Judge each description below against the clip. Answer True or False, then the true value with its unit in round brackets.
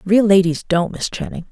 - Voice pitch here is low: False (190 Hz)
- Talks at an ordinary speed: True (195 wpm)